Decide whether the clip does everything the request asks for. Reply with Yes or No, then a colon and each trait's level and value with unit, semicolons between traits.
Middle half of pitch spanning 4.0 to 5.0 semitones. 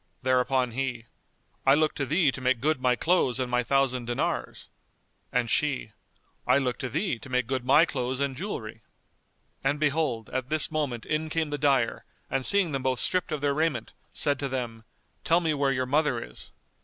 No: average, 3.1 semitones